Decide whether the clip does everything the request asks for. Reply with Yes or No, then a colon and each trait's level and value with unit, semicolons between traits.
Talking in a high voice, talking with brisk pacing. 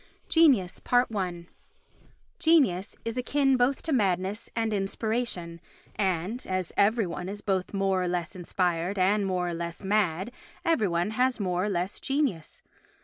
No: high, 195 Hz; average, 145 wpm